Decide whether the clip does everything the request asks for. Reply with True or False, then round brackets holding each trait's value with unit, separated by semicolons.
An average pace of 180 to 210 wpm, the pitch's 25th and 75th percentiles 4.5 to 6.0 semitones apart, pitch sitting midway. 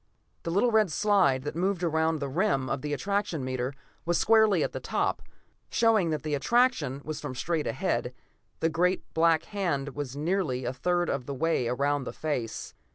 True (185 wpm; 5.3 semitones; 160 Hz)